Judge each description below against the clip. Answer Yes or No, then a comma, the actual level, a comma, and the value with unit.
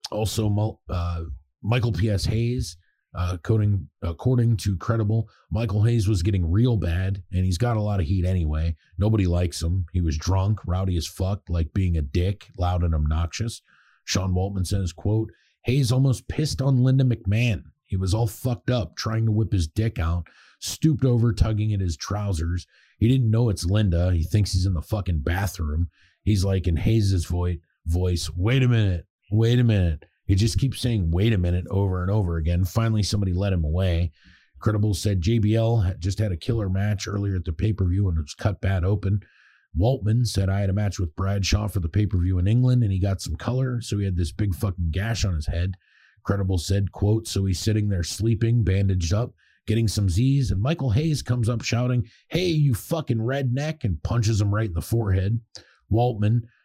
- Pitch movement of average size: Yes, average, 3.9 semitones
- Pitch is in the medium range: No, low, 100 Hz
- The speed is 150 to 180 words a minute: No, average, 200 wpm